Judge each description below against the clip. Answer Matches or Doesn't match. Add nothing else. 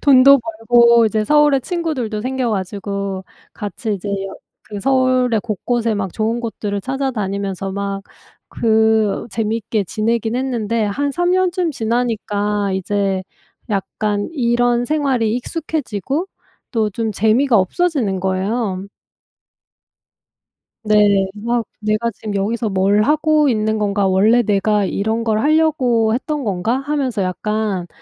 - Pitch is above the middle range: Matches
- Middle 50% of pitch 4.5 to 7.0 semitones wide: Doesn't match